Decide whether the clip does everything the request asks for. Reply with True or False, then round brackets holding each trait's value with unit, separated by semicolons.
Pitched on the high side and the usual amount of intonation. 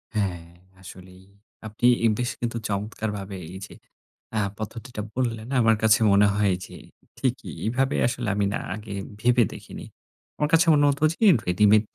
False (110 Hz; 3.3 semitones)